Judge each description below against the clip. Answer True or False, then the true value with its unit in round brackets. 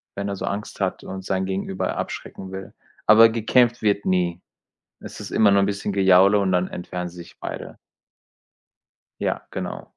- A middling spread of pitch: False (1.7 semitones)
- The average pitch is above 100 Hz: False (95 Hz)